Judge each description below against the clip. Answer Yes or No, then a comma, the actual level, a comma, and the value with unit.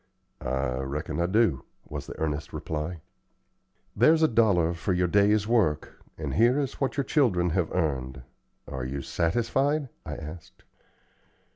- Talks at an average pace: Yes, average, 145 wpm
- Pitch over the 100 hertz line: No, very low, 85 Hz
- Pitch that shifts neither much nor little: No, wide, 7.5 semitones